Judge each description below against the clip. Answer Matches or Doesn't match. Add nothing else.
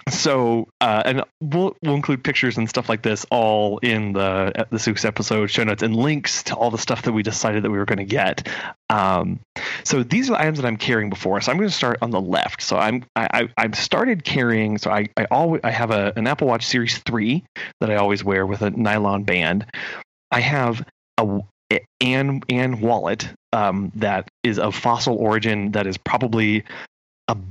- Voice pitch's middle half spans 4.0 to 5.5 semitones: Doesn't match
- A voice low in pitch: Matches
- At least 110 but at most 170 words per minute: Doesn't match